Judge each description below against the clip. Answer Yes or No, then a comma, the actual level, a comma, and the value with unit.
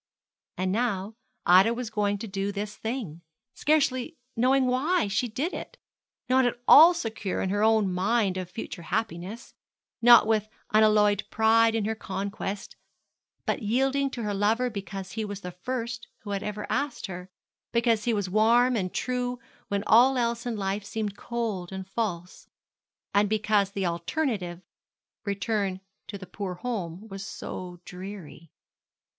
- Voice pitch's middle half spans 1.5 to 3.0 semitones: No, average, 3.4 semitones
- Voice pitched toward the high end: Yes, high, 210 Hz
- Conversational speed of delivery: Yes, average, 155 wpm